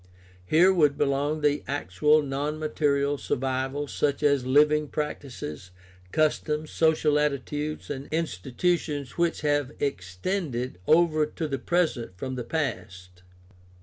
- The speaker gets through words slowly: Yes, slow, 120 wpm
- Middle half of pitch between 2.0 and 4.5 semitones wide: Yes, average, 2.9 semitones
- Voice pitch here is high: No, medium, 145 Hz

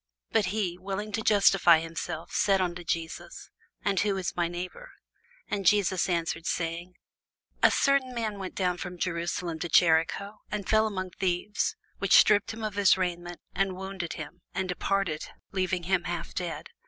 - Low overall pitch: No, medium, 185 Hz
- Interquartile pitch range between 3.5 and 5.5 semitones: No, narrow, 2.5 semitones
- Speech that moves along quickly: No, average, 165 wpm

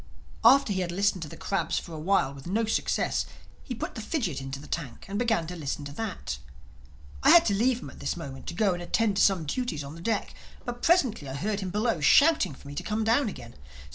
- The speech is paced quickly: Yes, fast, 245 wpm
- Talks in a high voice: Yes, high, 195 Hz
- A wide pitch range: Yes, wide, 6.5 semitones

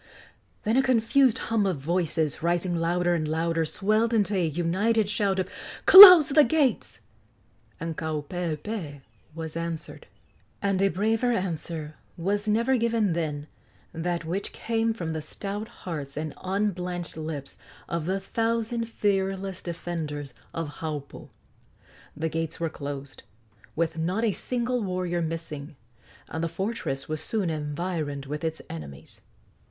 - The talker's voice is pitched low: No, medium, 175 Hz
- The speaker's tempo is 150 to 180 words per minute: No, slow, 135 wpm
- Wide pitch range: No, average, 4.9 semitones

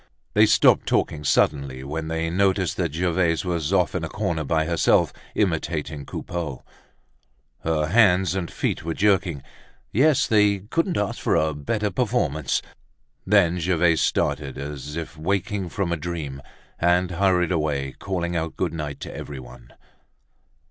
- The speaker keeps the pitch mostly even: No, average, 3.6 semitones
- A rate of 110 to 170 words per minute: Yes, average, 145 wpm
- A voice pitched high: No, very low, 85 Hz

